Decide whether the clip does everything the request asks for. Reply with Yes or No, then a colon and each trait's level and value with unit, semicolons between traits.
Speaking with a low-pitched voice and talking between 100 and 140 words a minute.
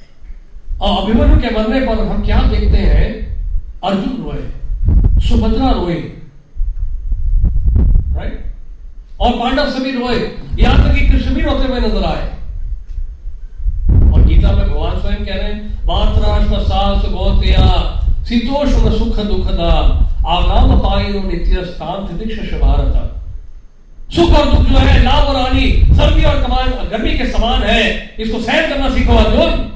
Yes: very low, 90 Hz; average, 130 wpm